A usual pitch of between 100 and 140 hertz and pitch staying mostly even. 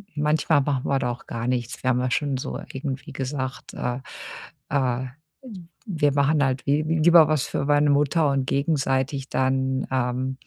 Yes: low, 135 Hz; narrow, 2.2 semitones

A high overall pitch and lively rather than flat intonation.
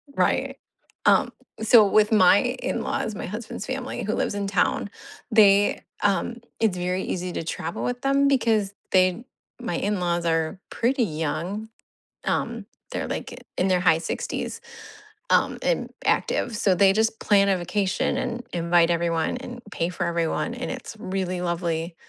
No: high, 195 Hz; average, 4.6 semitones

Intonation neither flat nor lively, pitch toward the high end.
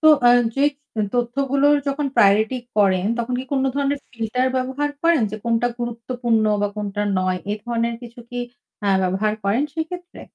Yes: average, 4.3 semitones; high, 240 Hz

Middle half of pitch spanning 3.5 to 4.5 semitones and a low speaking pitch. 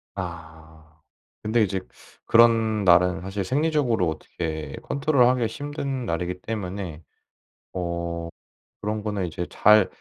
No: average, 5.1 semitones; very low, 95 Hz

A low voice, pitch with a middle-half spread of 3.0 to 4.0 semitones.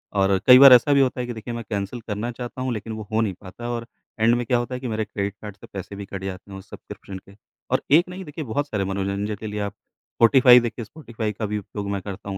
Yes: low, 110 Hz; average, 3.5 semitones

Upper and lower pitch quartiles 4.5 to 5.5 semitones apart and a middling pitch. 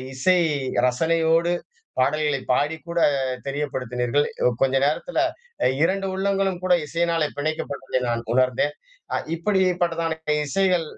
No: average, 3.9 semitones; medium, 160 Hz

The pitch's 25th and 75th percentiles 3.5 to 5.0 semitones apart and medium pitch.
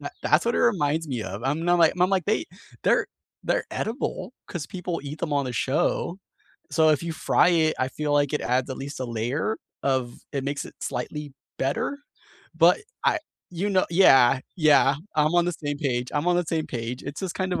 Yes: average, 4.6 semitones; medium, 150 Hz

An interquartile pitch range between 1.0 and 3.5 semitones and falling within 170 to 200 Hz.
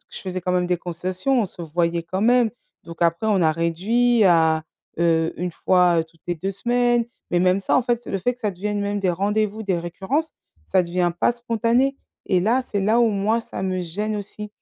No: average, 4.2 semitones; high, 190 Hz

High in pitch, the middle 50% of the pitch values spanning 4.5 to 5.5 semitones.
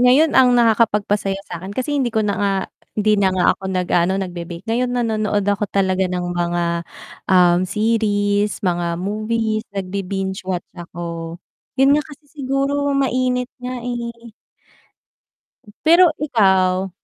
Yes: high, 205 Hz; average, 5.0 semitones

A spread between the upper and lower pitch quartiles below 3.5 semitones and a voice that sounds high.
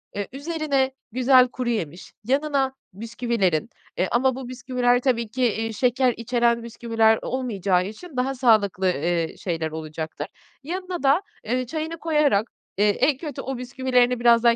No: average, 3.8 semitones; high, 245 Hz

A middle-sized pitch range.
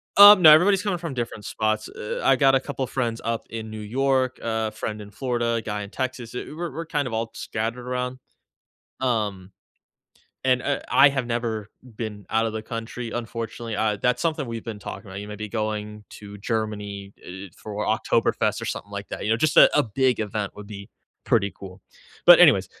Yes: average, 3.3 semitones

